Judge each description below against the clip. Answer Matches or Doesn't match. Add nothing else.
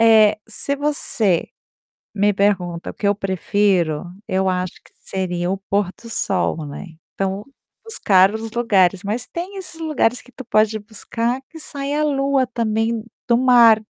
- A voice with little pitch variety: Doesn't match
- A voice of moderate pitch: Doesn't match